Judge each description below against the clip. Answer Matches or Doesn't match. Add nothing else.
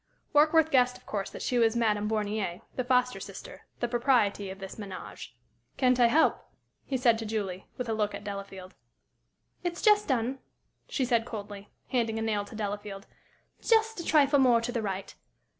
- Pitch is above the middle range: Matches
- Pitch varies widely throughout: Doesn't match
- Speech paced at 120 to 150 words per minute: Doesn't match